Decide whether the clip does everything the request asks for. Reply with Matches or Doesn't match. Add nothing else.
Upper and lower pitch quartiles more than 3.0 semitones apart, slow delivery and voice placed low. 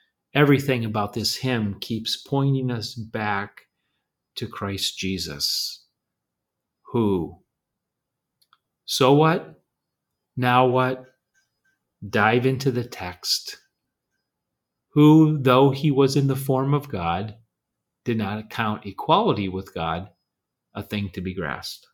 Matches